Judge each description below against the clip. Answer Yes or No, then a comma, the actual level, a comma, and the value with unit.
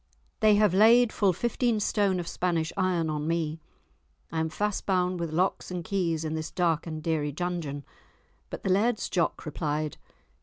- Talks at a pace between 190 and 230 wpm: No, average, 175 wpm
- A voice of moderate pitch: Yes, medium, 175 Hz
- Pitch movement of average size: Yes, average, 3.7 semitones